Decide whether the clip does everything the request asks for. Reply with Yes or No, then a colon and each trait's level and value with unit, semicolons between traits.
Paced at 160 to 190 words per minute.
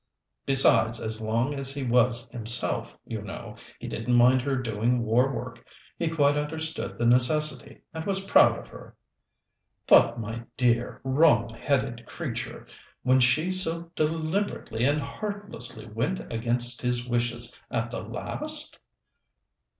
No: slow, 135 wpm